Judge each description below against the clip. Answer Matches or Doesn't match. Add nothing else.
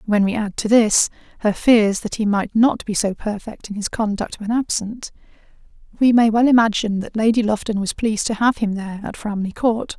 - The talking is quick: Matches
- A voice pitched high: Matches